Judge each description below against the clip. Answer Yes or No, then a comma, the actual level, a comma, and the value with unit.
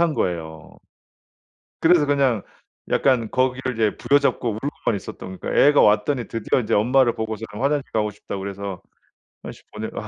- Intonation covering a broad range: No, average, 4.8 semitones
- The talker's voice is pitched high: No, low, 115 Hz